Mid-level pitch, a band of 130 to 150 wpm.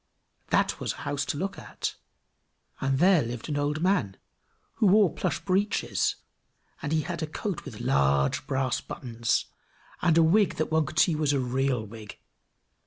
No: medium, 145 Hz; average, 175 wpm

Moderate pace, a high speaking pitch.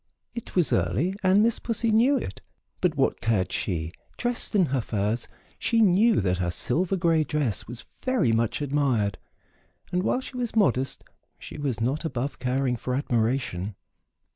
No: average, 165 wpm; medium, 140 Hz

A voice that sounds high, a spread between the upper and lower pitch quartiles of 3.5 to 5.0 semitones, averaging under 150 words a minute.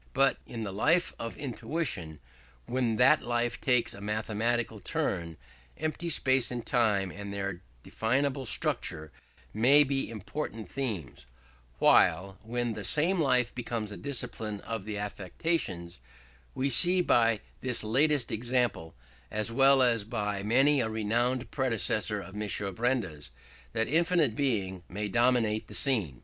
No: low, 115 Hz; average, 4.1 semitones; slow, 135 wpm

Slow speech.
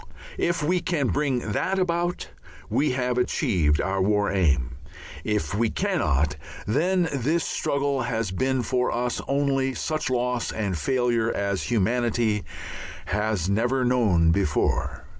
Yes: slow, 130 wpm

